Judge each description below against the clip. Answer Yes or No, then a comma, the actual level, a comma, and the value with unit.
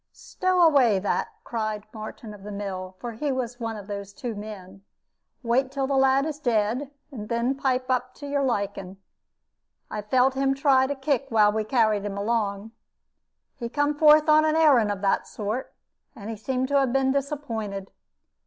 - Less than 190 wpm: Yes, average, 180 wpm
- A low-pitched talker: No, high, 240 Hz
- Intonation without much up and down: No, average, 4.6 semitones